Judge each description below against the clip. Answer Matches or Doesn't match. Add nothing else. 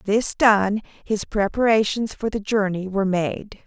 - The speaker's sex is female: Matches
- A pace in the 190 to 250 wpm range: Doesn't match